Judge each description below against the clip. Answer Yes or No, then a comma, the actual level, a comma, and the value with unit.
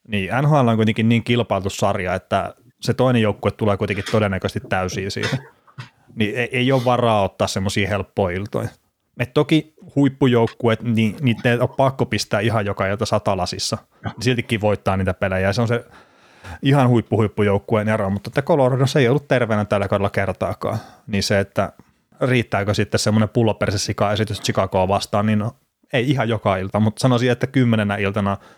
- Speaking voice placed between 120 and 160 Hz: No, low, 110 Hz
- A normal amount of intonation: Yes, average, 3.3 semitones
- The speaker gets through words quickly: Yes, fast, 170 wpm